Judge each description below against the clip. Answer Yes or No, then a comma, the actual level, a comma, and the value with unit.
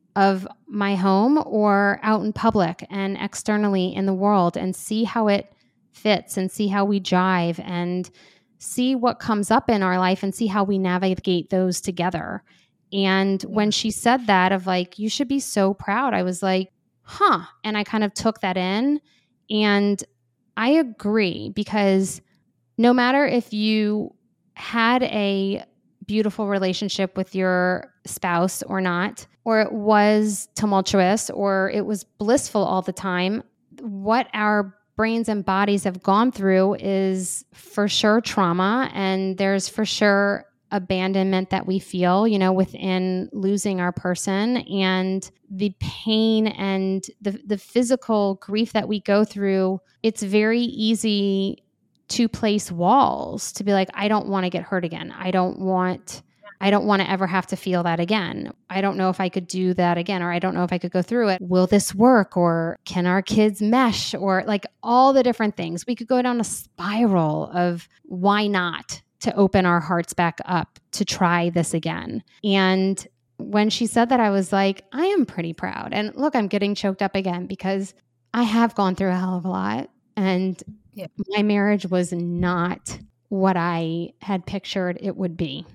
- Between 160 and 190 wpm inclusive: Yes, average, 175 wpm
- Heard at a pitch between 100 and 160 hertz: No, high, 195 Hz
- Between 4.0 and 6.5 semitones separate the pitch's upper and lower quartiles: No, narrow, 2.5 semitones